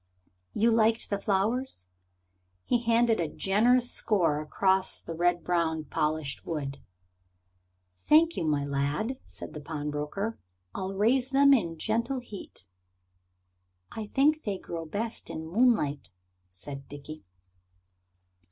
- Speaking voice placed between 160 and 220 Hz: Yes, high, 190 Hz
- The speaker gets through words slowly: Yes, slow, 120 wpm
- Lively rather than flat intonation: Yes, wide, 7.3 semitones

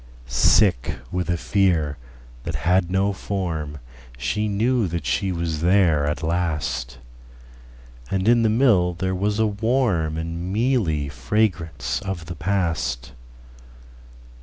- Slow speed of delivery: Yes, slow, 110 wpm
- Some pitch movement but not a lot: No, wide, 5.9 semitones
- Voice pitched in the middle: No, very low, 85 Hz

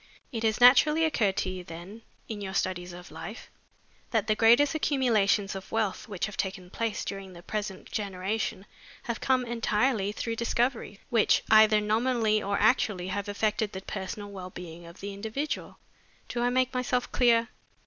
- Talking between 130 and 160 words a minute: No, average, 170 wpm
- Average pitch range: Yes, average, 3.5 semitones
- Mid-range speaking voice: No, high, 215 Hz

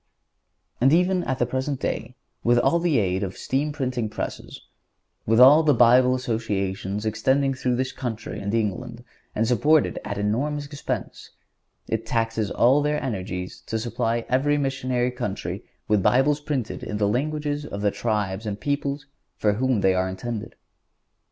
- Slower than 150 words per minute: No, average, 160 wpm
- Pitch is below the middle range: Yes, low, 120 Hz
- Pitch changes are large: No, average, 4.6 semitones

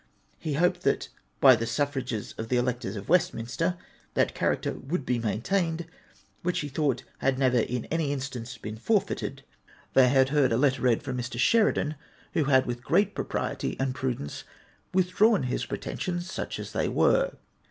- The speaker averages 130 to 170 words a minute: Yes, average, 165 wpm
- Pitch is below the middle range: Yes, low, 130 Hz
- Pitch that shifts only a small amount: No, average, 5.1 semitones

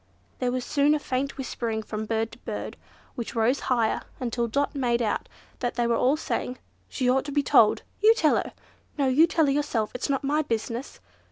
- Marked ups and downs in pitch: No, average, 3.4 semitones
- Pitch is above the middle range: Yes, very high, 255 Hz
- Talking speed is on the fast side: Yes, fast, 215 wpm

